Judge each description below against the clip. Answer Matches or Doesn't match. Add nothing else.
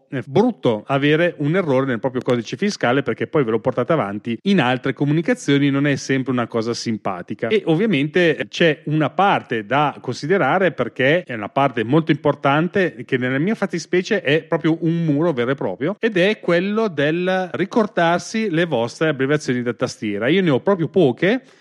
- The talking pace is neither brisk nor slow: Doesn't match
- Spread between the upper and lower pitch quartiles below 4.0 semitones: Doesn't match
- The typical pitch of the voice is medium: Matches